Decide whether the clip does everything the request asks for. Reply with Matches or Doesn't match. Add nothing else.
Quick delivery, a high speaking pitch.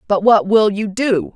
Matches